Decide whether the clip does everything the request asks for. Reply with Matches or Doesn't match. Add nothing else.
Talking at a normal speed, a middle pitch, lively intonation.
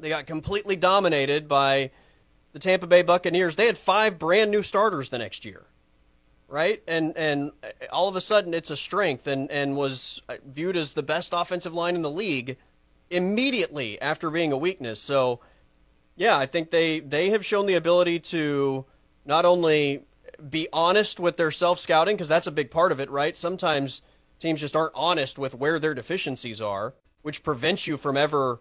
Doesn't match